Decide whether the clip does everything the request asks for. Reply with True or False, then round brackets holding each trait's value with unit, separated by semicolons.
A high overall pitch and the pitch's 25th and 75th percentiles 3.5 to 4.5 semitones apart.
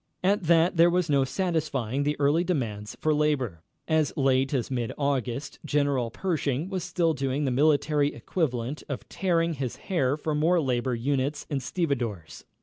False (145 Hz; 3.9 semitones)